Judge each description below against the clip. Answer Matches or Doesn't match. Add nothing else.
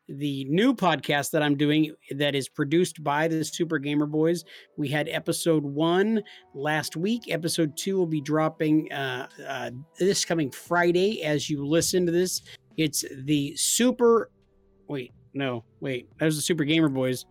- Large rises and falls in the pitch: Doesn't match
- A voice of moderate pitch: Matches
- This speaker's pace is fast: Doesn't match